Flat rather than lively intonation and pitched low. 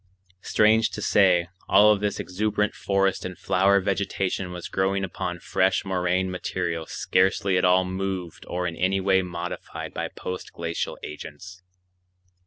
Yes: narrow, 1.4 semitones; very low, 95 Hz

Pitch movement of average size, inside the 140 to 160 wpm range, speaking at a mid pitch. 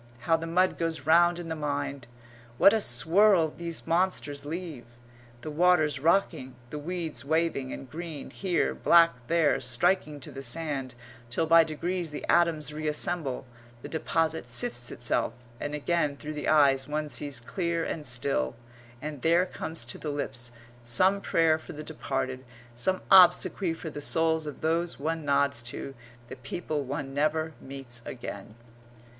Yes: average, 3.6 semitones; average, 155 wpm; medium, 155 Hz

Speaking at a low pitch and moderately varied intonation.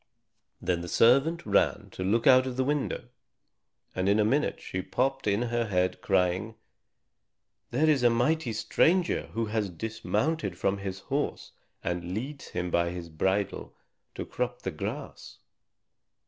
No: low, 110 Hz; wide, 5.8 semitones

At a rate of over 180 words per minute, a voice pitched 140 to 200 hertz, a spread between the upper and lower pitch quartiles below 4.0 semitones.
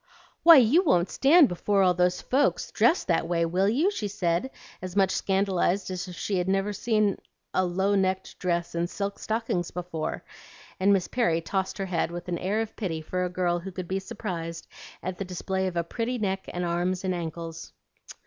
Yes: average, 195 wpm; medium, 185 Hz; narrow, 2.5 semitones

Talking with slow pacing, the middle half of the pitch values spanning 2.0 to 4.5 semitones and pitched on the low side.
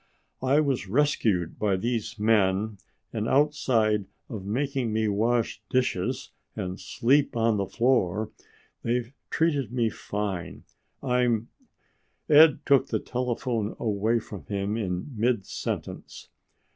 Yes: slow, 120 wpm; average, 3.7 semitones; low, 115 Hz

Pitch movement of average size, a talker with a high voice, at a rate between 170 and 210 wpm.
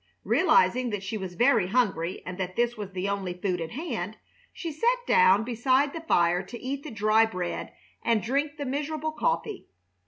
No: wide, 7.1 semitones; high, 235 Hz; average, 185 wpm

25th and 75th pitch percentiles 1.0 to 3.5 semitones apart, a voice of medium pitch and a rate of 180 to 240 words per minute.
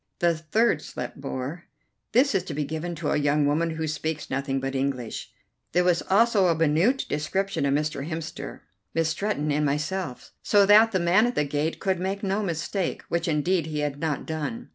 No: average, 4.3 semitones; medium, 160 Hz; average, 195 wpm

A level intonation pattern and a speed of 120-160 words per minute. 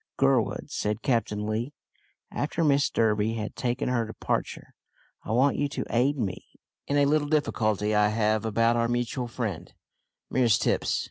No: average, 4.2 semitones; average, 155 wpm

